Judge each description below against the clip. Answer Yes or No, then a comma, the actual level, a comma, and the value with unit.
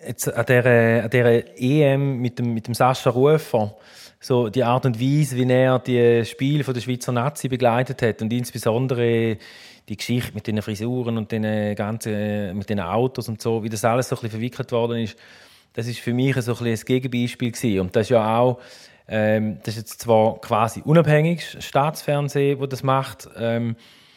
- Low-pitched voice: Yes, low, 120 Hz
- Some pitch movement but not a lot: No, narrow, 2.3 semitones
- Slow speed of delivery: No, average, 185 wpm